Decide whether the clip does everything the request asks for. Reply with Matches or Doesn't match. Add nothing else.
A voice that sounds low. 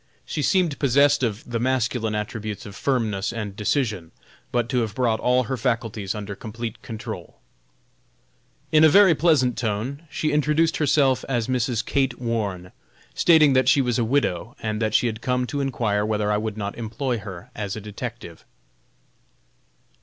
Matches